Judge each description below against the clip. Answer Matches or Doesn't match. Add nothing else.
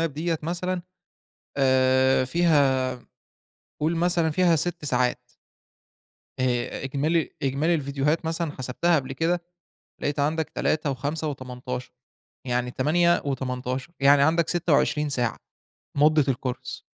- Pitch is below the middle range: Doesn't match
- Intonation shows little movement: Doesn't match